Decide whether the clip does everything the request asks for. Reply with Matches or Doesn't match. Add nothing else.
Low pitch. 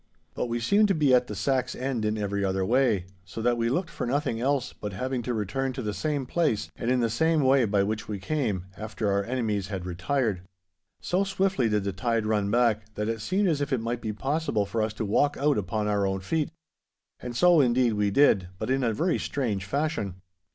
Matches